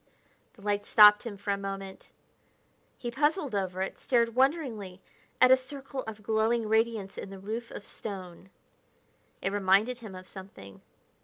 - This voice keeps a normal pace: Yes, average, 155 wpm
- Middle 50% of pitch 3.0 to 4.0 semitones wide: Yes, average, 3.4 semitones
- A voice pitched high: Yes, high, 210 Hz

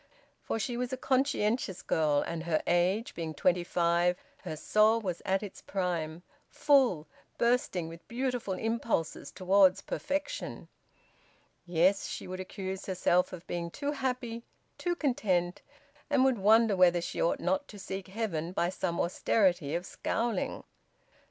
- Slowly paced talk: No, average, 145 wpm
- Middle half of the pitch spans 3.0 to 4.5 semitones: No, average, 5.0 semitones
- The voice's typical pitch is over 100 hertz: Yes, high, 190 Hz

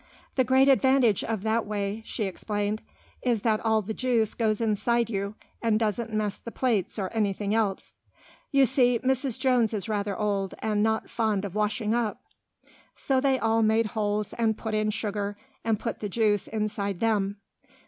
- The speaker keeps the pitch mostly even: Yes, narrow, 2.0 semitones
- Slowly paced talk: No, average, 175 wpm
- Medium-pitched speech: No, high, 220 Hz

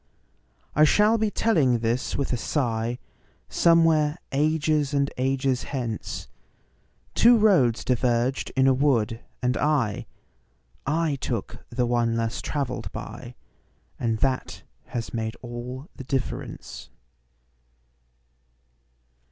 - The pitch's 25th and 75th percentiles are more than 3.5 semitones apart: Yes, average, 4.0 semitones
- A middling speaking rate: No, slow, 95 wpm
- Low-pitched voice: Yes, low, 130 Hz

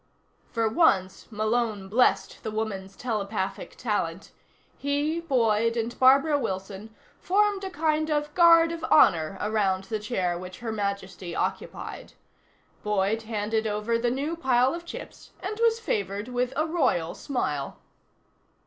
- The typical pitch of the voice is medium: No, high, 225 Hz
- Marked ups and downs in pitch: Yes, wide, 6.8 semitones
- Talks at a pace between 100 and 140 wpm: Yes, slow, 135 wpm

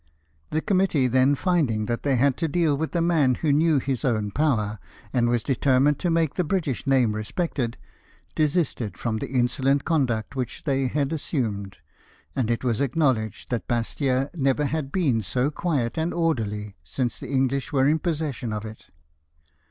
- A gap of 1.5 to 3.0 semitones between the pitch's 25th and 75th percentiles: No, average, 4.6 semitones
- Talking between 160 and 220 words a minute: Yes, average, 170 wpm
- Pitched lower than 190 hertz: Yes, low, 135 Hz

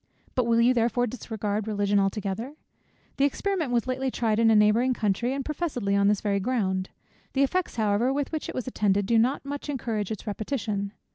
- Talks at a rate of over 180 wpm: Yes, average, 195 wpm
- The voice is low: No, high, 230 Hz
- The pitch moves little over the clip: No, average, 4.0 semitones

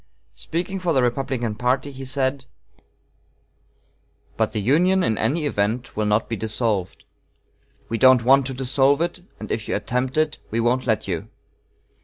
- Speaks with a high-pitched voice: No, low, 130 Hz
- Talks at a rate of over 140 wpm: Yes, average, 160 wpm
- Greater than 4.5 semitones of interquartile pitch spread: No, average, 3.8 semitones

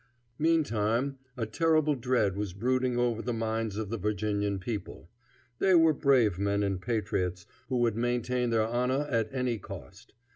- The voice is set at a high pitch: No, low, 115 Hz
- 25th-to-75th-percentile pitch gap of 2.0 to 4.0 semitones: Yes, average, 3.6 semitones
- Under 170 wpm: Yes, average, 155 wpm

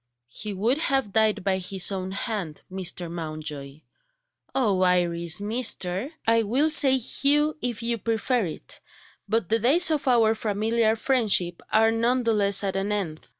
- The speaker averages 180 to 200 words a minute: No, average, 160 wpm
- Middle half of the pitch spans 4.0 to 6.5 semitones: Yes, average, 4.4 semitones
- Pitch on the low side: No, high, 215 Hz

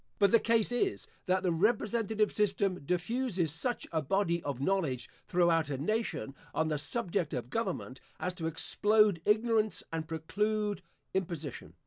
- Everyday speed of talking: Yes, average, 145 wpm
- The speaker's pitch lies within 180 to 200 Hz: Yes, medium, 185 Hz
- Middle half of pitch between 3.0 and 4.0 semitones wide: No, average, 4.9 semitones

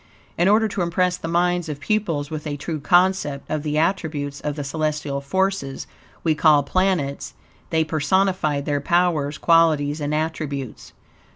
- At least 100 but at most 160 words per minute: Yes, average, 155 wpm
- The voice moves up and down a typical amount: Yes, average, 3.5 semitones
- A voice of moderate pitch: Yes, medium, 155 Hz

